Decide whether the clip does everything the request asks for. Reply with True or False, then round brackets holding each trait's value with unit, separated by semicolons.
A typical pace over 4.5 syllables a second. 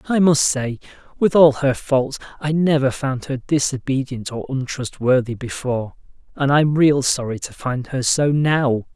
False (4.4 syllables/s)